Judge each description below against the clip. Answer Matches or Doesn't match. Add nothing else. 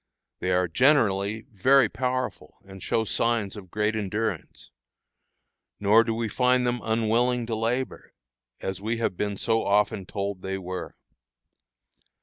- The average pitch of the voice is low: Matches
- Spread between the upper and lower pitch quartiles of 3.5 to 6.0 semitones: Doesn't match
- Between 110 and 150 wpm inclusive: Matches